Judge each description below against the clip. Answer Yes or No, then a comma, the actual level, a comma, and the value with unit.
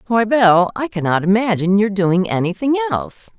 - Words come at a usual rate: Yes, average, 160 wpm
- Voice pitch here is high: Yes, high, 200 Hz